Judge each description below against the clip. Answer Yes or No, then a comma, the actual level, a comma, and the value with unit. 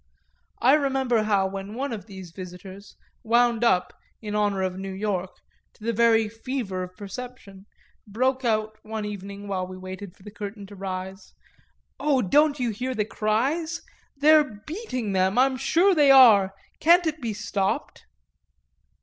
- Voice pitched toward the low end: No, high, 215 Hz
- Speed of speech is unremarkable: Yes, average, 160 wpm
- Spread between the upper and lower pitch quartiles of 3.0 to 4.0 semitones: No, average, 4.9 semitones